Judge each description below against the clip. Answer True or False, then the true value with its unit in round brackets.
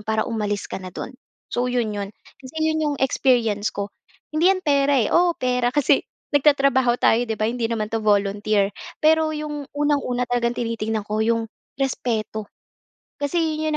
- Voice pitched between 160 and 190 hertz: False (245 Hz)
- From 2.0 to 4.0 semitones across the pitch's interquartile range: False (5.0 semitones)